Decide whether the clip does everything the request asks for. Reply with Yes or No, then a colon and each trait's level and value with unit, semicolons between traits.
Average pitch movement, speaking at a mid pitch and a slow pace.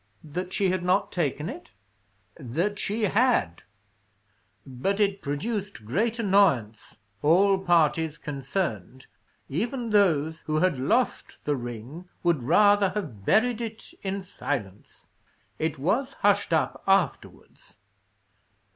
No: wide, 6.2 semitones; medium, 180 Hz; slow, 115 wpm